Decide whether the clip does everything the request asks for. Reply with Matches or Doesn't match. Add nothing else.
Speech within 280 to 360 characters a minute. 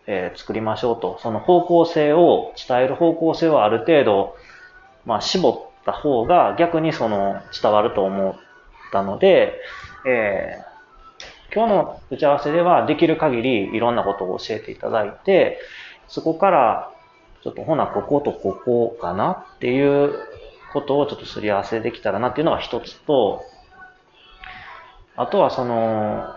Matches